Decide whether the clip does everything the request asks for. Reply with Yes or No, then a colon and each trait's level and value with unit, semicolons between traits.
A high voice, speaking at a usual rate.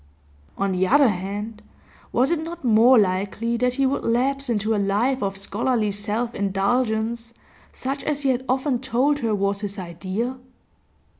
Yes: high, 230 Hz; average, 160 wpm